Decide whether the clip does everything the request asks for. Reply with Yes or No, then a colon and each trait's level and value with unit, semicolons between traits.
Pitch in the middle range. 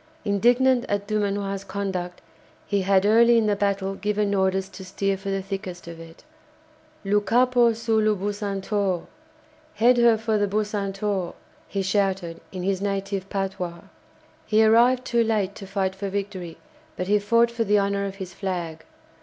No: high, 200 Hz